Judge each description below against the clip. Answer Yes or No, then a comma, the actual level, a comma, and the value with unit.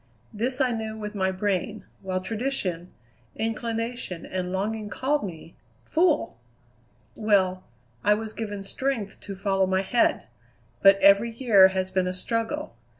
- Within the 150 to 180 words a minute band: No, average, 140 wpm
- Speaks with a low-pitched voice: No, high, 210 Hz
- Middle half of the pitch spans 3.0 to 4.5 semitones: Yes, average, 3.3 semitones